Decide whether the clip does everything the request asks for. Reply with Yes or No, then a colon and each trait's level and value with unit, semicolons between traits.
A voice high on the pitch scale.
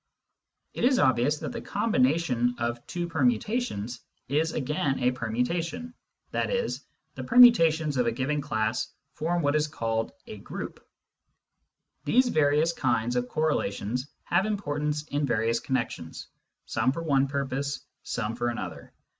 No: medium, 140 Hz